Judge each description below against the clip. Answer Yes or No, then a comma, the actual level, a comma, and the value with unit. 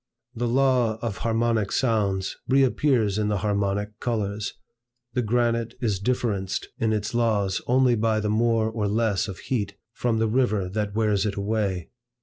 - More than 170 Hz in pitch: No, low, 110 Hz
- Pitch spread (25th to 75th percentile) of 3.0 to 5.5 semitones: No, narrow, 2.5 semitones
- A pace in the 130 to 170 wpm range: Yes, average, 155 wpm